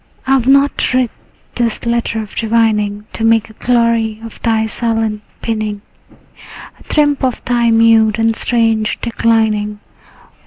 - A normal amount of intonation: No, narrow, 1.4 semitones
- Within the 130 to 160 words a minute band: Yes, average, 140 wpm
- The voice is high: Yes, high, 225 Hz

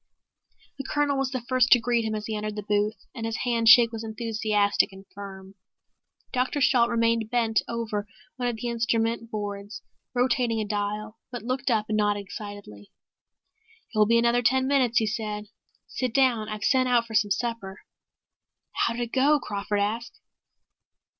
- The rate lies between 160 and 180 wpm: Yes, average, 175 wpm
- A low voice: No, high, 225 Hz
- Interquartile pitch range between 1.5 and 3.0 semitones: Yes, narrow, 2.6 semitones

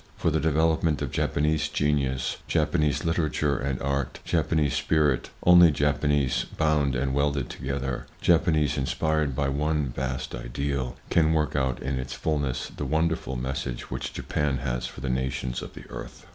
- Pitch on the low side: Yes, very low, 70 Hz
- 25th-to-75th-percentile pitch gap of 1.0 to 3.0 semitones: Yes, average, 2.7 semitones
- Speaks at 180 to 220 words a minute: No, average, 155 wpm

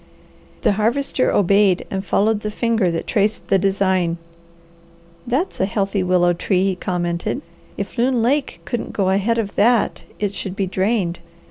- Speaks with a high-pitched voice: Yes, high, 200 Hz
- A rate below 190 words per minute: Yes, average, 155 wpm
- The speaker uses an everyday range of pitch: Yes, average, 3.2 semitones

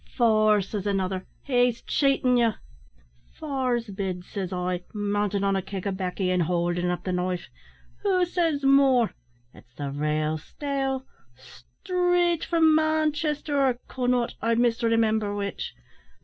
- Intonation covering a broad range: Yes, wide, 6.8 semitones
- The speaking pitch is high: Yes, high, 220 Hz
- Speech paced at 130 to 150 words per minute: Yes, slow, 135 wpm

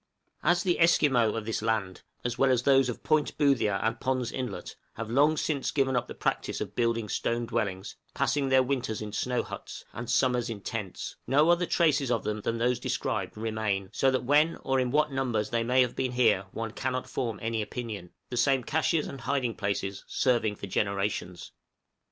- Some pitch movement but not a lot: Yes, average, 3.5 semitones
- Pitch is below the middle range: Yes, low, 120 Hz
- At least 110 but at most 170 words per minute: No, average, 195 wpm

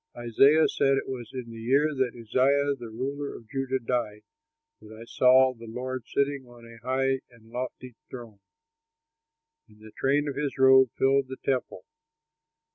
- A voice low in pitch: Yes, low, 130 Hz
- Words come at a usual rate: Yes, average, 165 wpm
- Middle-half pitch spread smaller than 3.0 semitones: Yes, narrow, 2.6 semitones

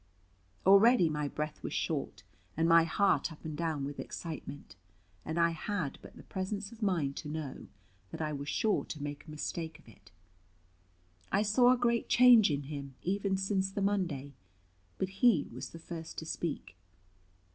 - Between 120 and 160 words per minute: No, average, 175 wpm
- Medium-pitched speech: Yes, medium, 165 Hz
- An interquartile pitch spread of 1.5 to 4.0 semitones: No, average, 5.0 semitones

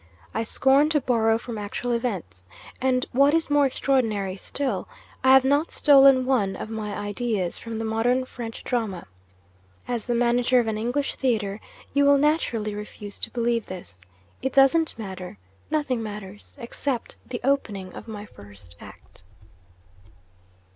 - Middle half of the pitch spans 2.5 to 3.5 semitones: No, average, 4.3 semitones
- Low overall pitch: No, high, 235 Hz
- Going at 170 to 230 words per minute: No, average, 150 wpm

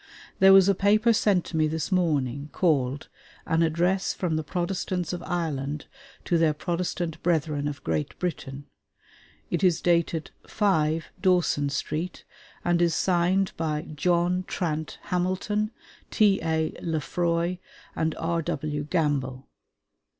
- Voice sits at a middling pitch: Yes, medium, 170 Hz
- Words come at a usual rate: No, slow, 125 wpm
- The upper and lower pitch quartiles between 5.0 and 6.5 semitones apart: No, average, 3.0 semitones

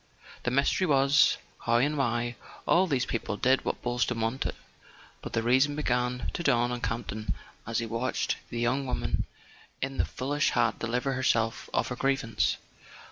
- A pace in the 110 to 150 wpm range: No, average, 165 wpm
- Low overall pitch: Yes, low, 125 Hz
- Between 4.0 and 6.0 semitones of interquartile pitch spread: No, narrow, 2.6 semitones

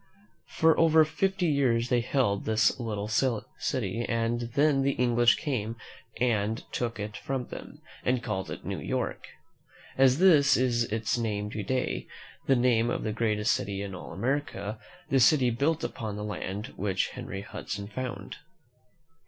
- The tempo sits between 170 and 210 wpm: No, average, 160 wpm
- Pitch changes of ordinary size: Yes, average, 3.9 semitones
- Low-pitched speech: Yes, low, 115 Hz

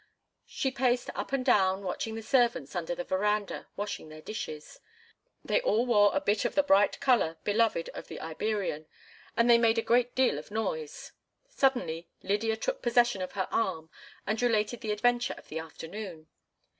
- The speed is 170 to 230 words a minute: Yes, average, 175 wpm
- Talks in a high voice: Yes, high, 215 Hz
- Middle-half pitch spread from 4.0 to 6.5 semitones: Yes, average, 4.5 semitones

